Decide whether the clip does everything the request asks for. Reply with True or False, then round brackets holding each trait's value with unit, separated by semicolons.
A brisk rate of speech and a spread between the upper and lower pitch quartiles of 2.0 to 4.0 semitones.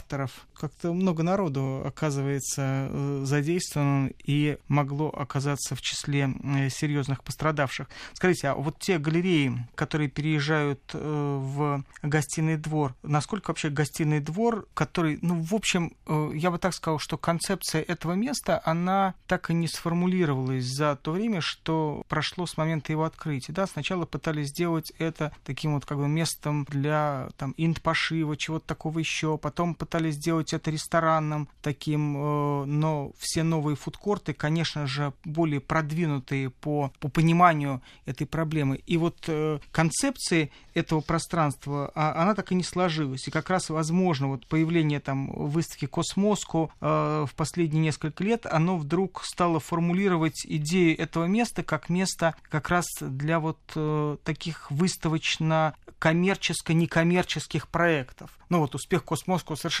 False (130 wpm; 2.5 semitones)